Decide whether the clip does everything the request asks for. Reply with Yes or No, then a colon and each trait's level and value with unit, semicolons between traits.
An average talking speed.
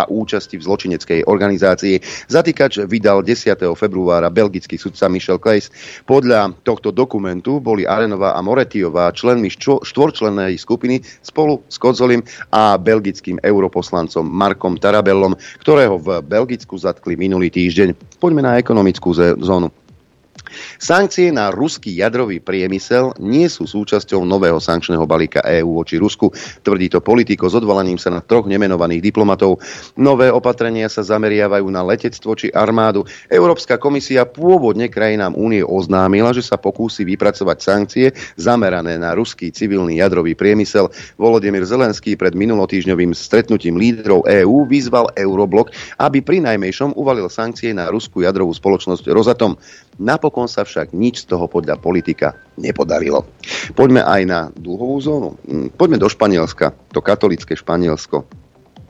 Yes: average, 135 wpm